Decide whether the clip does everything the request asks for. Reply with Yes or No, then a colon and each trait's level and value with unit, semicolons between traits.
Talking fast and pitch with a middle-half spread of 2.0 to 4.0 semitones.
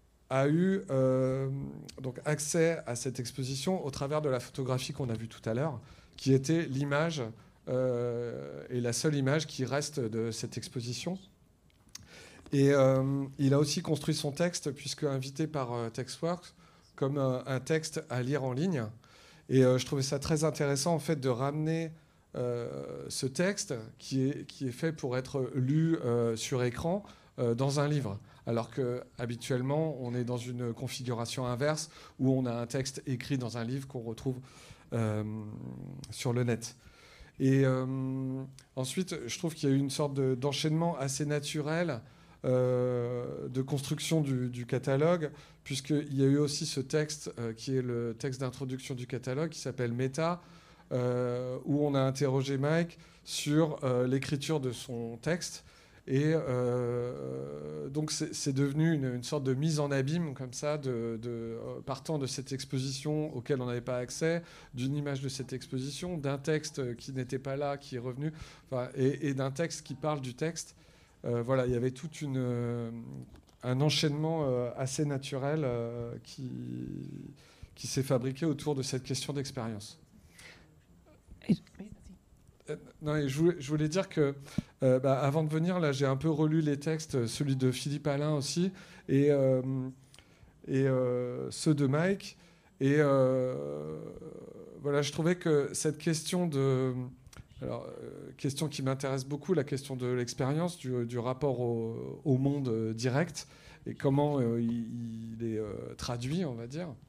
No: average, 165 wpm; average, 3.4 semitones